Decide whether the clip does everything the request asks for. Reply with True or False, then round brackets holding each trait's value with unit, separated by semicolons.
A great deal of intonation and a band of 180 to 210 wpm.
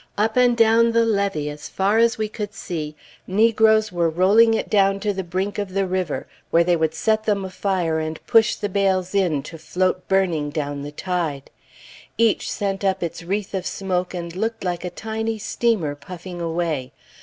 False (3.9 semitones; 190 wpm)